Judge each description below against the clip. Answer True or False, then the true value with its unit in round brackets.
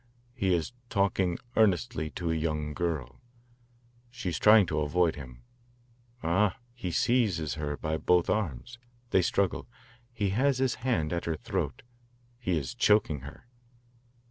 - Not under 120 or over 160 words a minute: True (145 wpm)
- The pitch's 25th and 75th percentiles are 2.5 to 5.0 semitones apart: False (5.4 semitones)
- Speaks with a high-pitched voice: False (85 Hz)